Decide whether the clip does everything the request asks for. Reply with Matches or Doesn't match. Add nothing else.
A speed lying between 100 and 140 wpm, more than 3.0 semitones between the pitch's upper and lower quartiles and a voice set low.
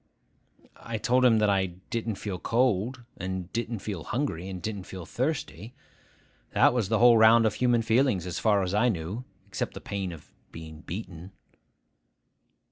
Doesn't match